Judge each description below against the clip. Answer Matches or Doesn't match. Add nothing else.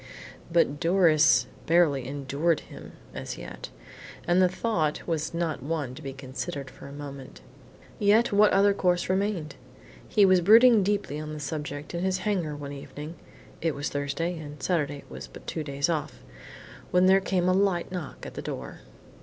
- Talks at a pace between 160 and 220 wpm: Matches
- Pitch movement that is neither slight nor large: Matches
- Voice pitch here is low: Doesn't match